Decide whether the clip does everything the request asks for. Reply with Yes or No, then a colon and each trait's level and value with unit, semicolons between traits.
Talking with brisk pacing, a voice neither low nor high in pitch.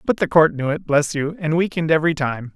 Yes: fast, 260 wpm; medium, 155 Hz